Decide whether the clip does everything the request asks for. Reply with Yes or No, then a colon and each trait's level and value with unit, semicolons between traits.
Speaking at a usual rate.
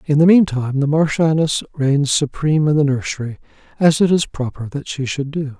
Yes: average, 180 wpm